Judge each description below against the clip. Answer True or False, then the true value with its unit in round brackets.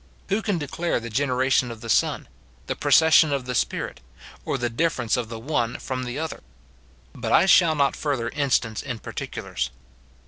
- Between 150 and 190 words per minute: True (175 wpm)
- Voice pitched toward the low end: True (130 Hz)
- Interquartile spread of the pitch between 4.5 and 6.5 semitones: True (4.9 semitones)